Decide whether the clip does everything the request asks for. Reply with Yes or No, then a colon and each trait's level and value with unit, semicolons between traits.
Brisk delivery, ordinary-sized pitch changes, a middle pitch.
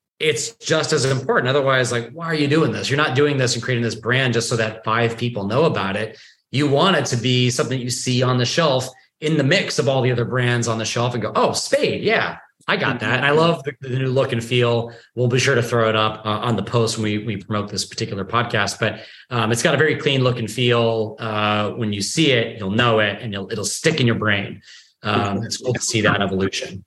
No: fast, 255 wpm; average, 3.4 semitones; low, 120 Hz